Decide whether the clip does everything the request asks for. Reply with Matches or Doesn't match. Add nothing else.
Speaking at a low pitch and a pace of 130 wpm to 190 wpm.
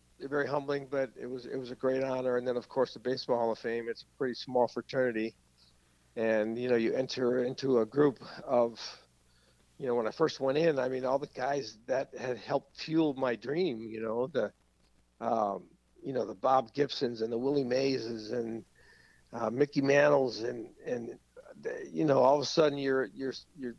Doesn't match